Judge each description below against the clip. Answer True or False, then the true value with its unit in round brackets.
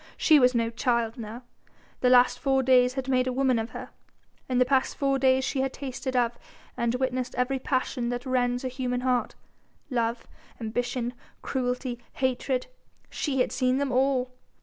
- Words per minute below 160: False (170 wpm)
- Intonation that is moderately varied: False (1.2 semitones)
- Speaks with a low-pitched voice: False (255 Hz)